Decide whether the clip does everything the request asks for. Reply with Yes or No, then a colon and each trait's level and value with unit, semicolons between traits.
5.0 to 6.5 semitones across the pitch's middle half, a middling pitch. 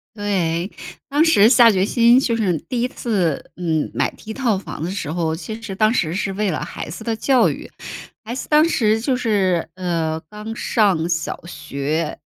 No: average, 5.3 semitones; high, 200 Hz